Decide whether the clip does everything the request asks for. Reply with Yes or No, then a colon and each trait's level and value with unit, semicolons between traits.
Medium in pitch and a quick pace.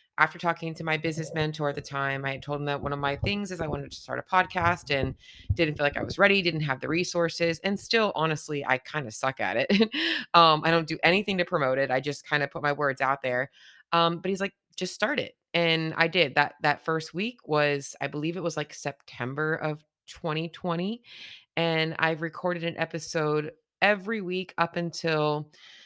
Yes: medium, 160 Hz; fast, 220 wpm